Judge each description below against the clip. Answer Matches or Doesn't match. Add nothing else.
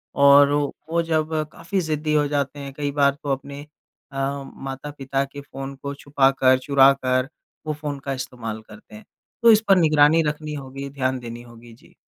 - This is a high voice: Doesn't match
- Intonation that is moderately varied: Doesn't match